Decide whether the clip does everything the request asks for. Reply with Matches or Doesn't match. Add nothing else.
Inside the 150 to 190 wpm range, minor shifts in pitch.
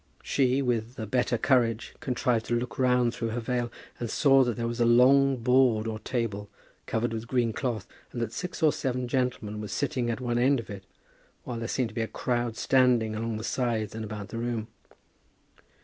Doesn't match